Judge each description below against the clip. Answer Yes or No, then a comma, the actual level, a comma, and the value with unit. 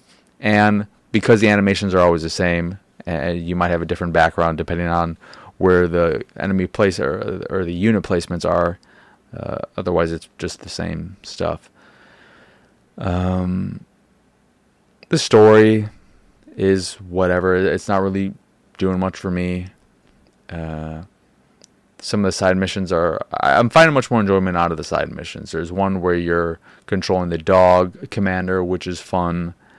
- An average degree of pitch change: No, narrow, 2.2 semitones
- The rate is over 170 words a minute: No, average, 150 wpm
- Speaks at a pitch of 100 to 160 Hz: No, very low, 90 Hz